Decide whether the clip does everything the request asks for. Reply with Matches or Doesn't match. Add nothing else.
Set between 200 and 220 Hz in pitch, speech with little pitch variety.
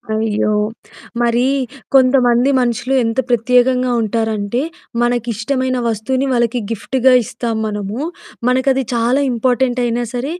Doesn't match